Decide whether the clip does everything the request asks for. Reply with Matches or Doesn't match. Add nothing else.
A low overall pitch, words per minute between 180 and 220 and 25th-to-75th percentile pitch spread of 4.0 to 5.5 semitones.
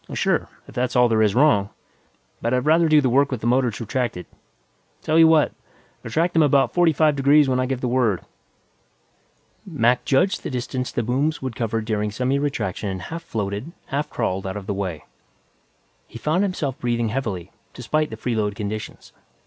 Matches